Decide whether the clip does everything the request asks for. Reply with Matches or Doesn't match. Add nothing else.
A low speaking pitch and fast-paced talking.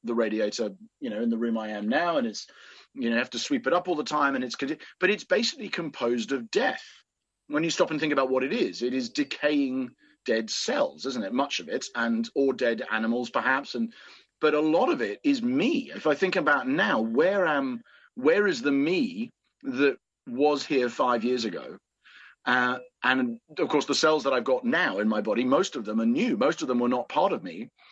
Doesn't match